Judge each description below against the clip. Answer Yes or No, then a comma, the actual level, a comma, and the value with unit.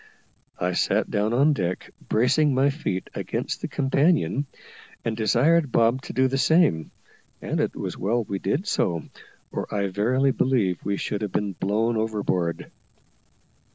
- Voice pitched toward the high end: No, low, 115 Hz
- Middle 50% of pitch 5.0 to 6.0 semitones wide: Yes, average, 5.3 semitones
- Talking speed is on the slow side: No, average, 155 wpm